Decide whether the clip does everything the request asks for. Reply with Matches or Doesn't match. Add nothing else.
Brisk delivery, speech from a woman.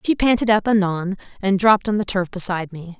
Matches